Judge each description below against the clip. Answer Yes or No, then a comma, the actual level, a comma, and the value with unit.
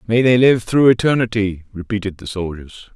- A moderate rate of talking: Yes, average, 160 wpm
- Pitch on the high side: No, low, 105 Hz